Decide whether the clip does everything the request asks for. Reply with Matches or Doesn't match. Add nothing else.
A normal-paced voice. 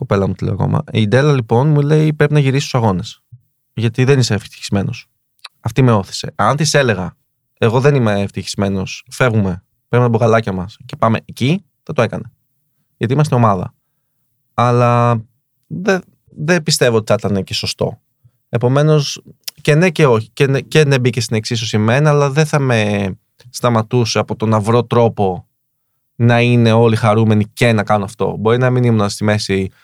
Doesn't match